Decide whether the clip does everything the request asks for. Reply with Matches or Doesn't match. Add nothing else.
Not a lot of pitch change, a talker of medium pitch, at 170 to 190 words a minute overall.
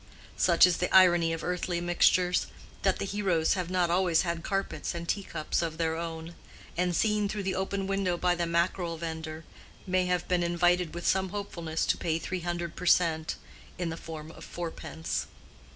Matches